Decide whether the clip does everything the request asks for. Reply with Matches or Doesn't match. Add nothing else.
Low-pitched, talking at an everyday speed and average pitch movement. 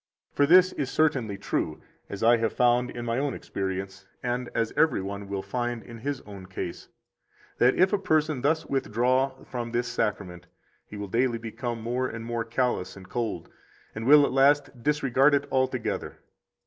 Matches